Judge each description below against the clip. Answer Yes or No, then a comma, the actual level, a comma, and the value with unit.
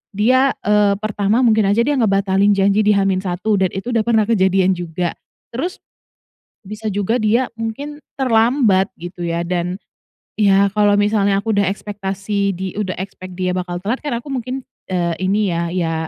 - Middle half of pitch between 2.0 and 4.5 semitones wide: Yes, average, 2.9 semitones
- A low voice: No, high, 200 Hz